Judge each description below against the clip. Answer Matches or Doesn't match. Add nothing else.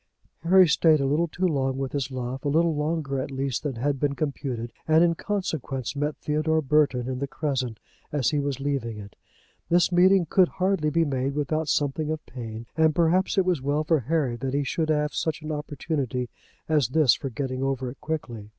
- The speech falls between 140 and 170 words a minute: Doesn't match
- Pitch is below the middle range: Doesn't match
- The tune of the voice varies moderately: Matches